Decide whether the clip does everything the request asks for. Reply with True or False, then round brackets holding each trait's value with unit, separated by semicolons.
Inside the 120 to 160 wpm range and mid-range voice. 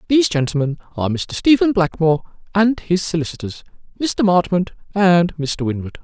True (140 wpm; 180 Hz)